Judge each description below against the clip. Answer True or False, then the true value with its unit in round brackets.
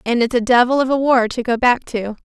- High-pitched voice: True (245 Hz)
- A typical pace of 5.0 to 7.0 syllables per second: True (5.8 syllables/s)